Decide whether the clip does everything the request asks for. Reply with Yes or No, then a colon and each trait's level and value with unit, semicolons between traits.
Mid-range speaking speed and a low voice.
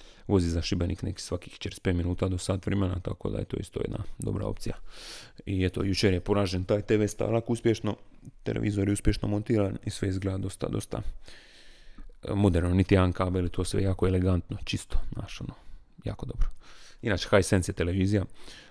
No: fast, 165 wpm; low, 100 Hz